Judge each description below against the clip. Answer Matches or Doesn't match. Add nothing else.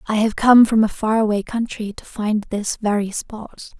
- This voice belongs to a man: Doesn't match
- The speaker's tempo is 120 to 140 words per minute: Doesn't match